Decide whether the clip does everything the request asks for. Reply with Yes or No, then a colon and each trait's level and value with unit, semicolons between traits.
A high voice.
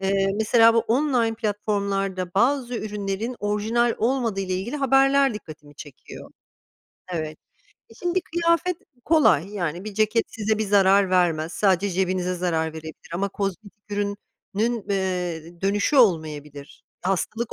Yes: high, 200 Hz